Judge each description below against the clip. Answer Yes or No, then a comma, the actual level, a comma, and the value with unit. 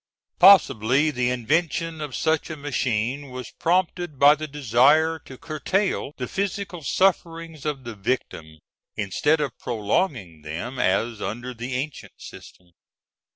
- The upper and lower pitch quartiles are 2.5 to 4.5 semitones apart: No, average, 5.2 semitones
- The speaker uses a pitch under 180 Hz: Yes, medium, 140 Hz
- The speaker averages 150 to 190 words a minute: No, slow, 135 wpm